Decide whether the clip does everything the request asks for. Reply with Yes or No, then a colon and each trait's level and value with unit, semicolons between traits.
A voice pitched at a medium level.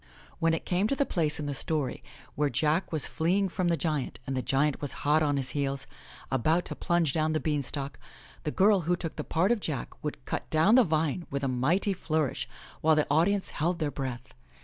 Yes: medium, 155 Hz